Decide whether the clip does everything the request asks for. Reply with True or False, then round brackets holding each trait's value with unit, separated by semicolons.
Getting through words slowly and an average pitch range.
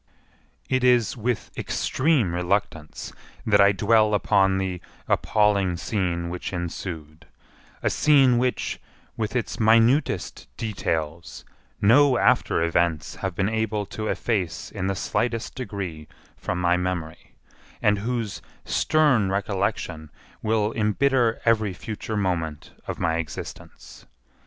True (120 wpm; 4.4 semitones)